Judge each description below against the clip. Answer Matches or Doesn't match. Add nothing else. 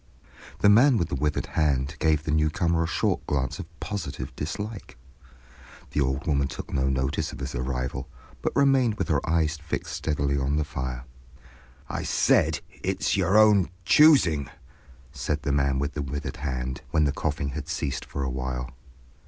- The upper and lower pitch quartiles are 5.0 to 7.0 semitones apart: Doesn't match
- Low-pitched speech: Matches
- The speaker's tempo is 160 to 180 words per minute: Matches